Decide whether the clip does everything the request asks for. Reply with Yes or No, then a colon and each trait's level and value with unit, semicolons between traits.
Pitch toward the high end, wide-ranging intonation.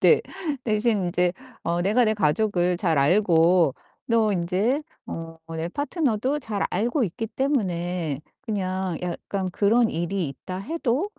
No: high, 195 Hz; average, 4.6 semitones